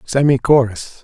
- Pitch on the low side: Yes, low, 130 Hz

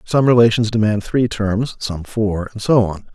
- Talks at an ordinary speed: Yes, average, 190 wpm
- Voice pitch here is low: Yes, low, 110 Hz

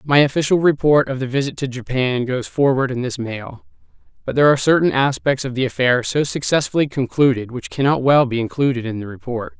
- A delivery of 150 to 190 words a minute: No, average, 200 wpm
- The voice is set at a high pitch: No, low, 130 Hz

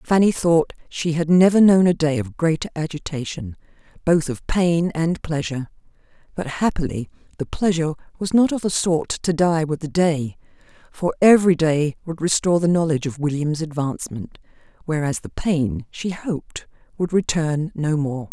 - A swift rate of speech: No, average, 160 wpm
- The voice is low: No, medium, 160 Hz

